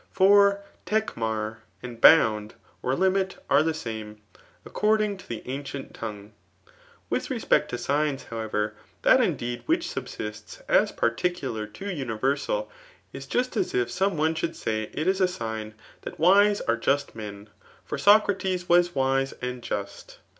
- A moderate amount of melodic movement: No, wide, 9.0 semitones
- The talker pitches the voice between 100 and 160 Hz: Yes, low, 135 Hz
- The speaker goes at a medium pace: Yes, average, 145 wpm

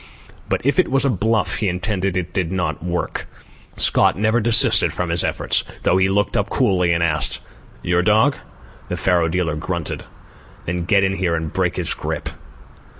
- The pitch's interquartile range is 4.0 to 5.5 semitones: No, average, 3.4 semitones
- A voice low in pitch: Yes, very low, 90 Hz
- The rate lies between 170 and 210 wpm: Yes, average, 180 wpm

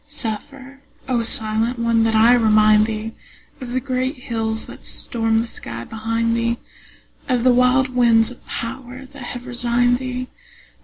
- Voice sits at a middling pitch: No, high, 235 Hz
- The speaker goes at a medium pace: Yes, average, 155 wpm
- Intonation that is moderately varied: No, narrow, 2.1 semitones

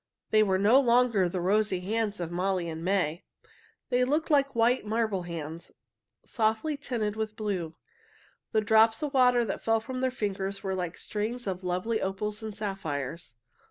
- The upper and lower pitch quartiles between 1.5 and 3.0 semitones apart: No, average, 3.8 semitones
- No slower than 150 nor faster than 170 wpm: Yes, average, 165 wpm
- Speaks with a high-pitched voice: Yes, high, 210 Hz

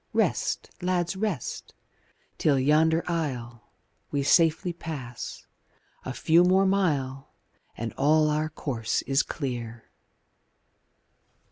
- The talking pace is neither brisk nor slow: No, slow, 100 wpm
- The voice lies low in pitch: No, medium, 150 Hz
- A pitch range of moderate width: Yes, average, 4.6 semitones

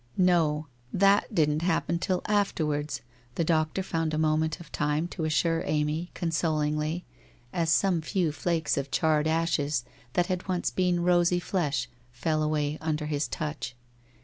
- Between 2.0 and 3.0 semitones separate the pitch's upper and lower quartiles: Yes, narrow, 2.5 semitones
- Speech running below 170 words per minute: Yes, average, 150 wpm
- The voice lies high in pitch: No, medium, 160 Hz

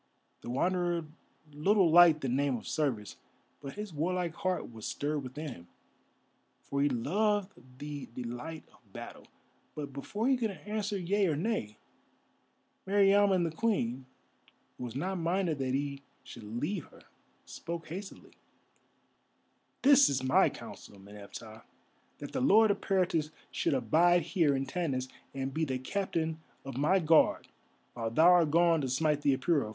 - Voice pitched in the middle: Yes, medium, 155 Hz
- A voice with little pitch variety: No, wide, 5.6 semitones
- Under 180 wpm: Yes, average, 150 wpm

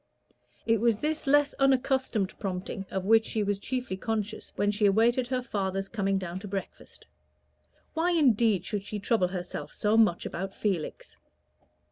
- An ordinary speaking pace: Yes, average, 155 wpm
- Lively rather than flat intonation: No, average, 4.0 semitones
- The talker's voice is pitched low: No, high, 210 Hz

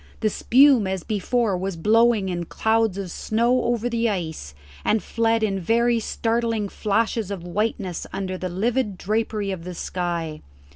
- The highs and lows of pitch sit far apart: No, average, 3.6 semitones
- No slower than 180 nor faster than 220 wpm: No, average, 155 wpm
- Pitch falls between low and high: No, high, 210 Hz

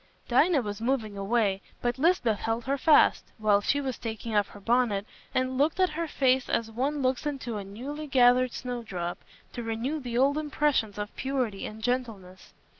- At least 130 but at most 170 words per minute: No, average, 180 wpm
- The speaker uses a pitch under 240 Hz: No, high, 245 Hz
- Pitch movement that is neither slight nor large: Yes, average, 4.1 semitones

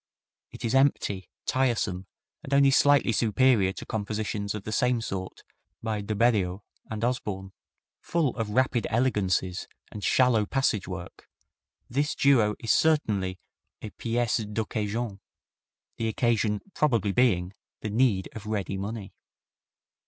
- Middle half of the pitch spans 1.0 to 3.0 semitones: No, average, 3.5 semitones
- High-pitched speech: No, low, 110 Hz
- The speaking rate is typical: No, slow, 130 wpm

